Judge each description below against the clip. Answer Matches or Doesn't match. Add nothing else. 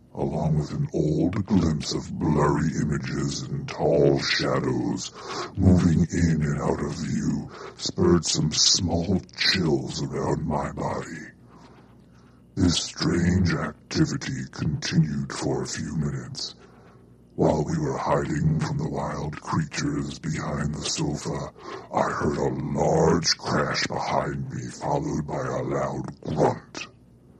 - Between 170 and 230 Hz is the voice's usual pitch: Doesn't match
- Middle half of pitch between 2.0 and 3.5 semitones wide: Matches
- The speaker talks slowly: Matches